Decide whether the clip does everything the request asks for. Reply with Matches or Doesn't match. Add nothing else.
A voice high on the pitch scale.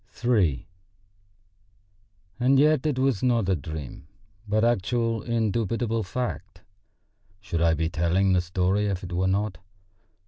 Doesn't match